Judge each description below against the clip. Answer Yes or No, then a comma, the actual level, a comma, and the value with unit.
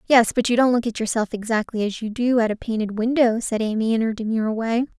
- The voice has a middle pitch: No, high, 230 Hz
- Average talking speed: No, fast, 255 wpm